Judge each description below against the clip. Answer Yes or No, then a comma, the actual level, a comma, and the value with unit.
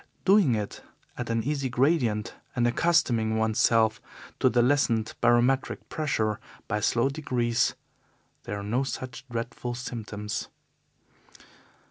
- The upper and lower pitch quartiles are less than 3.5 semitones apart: Yes, average, 3.1 semitones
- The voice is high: No, low, 120 Hz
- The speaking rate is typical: No, slow, 115 wpm